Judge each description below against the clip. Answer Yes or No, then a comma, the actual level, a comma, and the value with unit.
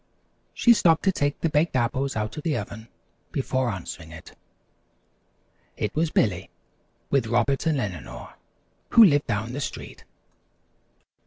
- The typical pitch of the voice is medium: No, low, 130 Hz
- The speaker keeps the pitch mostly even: No, wide, 5.6 semitones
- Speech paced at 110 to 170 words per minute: Yes, slow, 135 wpm